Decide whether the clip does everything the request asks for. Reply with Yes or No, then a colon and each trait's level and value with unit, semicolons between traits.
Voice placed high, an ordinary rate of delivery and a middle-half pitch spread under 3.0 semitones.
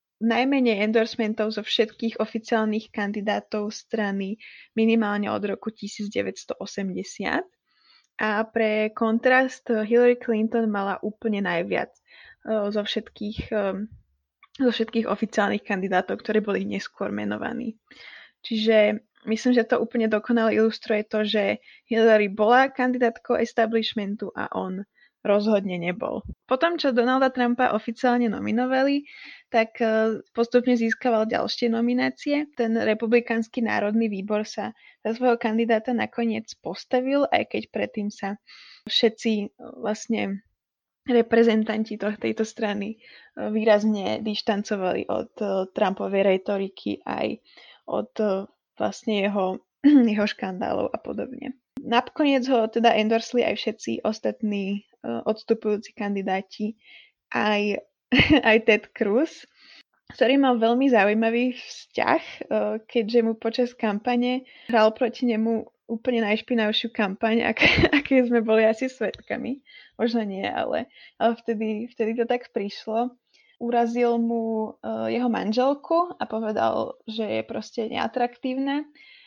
No: high, 225 Hz; slow, 105 wpm; narrow, 2.4 semitones